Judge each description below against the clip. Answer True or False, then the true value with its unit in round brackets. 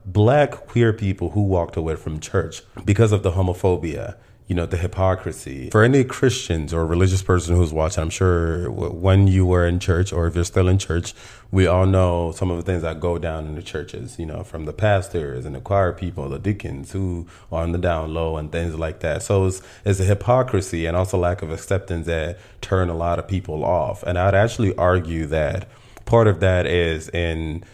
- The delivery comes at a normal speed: False (210 wpm)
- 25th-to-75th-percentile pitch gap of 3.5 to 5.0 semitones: False (2.8 semitones)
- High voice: False (90 Hz)